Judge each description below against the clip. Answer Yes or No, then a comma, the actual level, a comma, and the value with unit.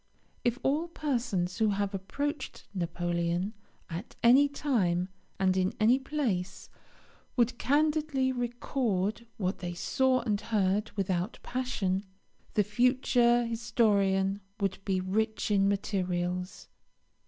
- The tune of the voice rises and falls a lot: No, average, 5.0 semitones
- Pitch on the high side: Yes, high, 210 Hz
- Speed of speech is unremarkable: No, slow, 110 wpm